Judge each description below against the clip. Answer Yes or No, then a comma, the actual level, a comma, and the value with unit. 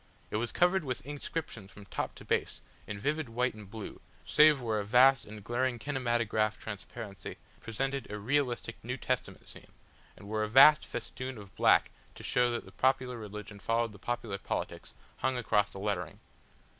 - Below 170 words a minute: No, average, 175 wpm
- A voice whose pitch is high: No, low, 120 Hz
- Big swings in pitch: No, average, 3.7 semitones